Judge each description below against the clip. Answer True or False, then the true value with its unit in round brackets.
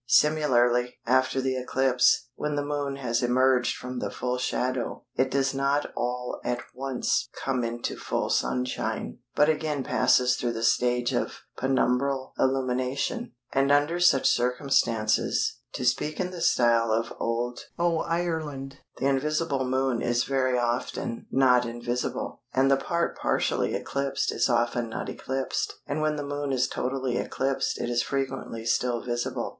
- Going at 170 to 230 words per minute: False (150 wpm)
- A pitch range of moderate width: False (2.1 semitones)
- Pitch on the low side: True (130 Hz)